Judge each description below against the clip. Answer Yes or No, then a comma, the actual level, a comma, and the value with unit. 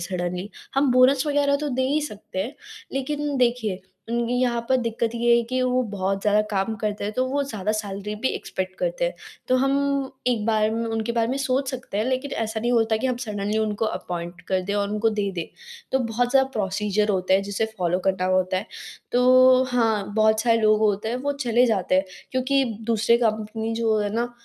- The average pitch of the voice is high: Yes, high, 225 Hz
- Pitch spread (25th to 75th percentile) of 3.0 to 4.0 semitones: Yes, average, 3.6 semitones